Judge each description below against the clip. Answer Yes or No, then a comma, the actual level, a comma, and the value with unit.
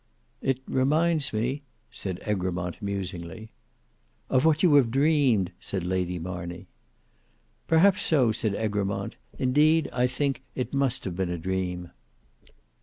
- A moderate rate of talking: No, slow, 125 wpm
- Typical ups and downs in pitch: No, wide, 7.1 semitones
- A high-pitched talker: No, low, 110 Hz